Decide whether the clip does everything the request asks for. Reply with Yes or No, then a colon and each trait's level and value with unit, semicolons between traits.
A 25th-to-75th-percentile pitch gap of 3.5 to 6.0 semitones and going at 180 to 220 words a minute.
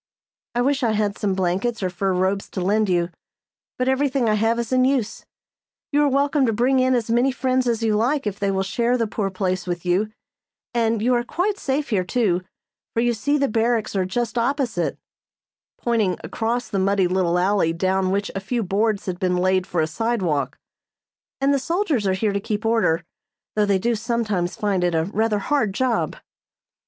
Yes: average, 4.3 semitones; average, 200 wpm